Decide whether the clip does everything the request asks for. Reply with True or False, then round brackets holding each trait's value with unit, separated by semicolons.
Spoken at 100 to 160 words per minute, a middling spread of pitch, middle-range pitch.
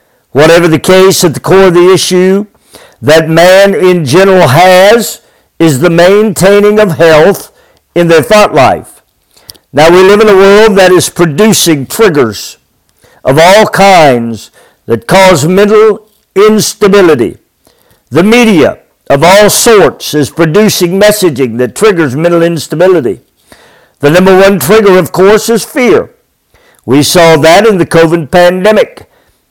True (135 wpm; 3.8 semitones; 180 Hz)